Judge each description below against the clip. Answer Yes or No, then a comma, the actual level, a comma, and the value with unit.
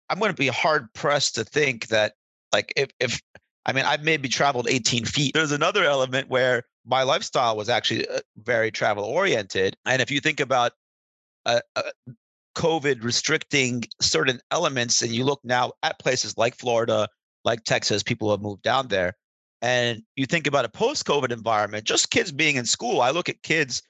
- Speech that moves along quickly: No, average, 180 wpm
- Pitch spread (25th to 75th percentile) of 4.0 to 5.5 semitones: No, average, 3.6 semitones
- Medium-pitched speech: No, low, 125 Hz